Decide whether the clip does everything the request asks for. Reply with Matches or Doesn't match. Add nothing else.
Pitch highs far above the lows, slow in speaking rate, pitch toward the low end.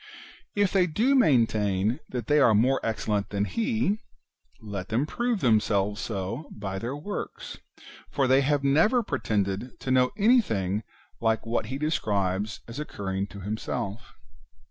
Doesn't match